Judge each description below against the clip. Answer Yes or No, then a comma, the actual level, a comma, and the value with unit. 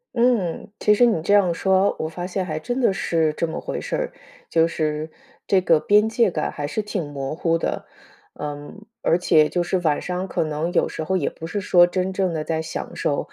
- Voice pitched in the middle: Yes, medium, 175 Hz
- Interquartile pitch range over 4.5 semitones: No, average, 3.6 semitones